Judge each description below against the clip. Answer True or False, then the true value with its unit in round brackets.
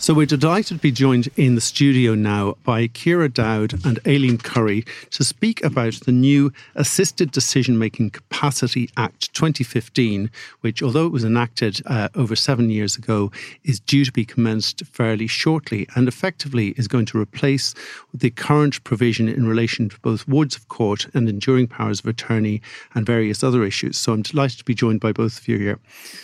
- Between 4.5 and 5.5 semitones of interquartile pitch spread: False (3.8 semitones)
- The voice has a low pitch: True (120 Hz)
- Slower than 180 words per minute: False (185 wpm)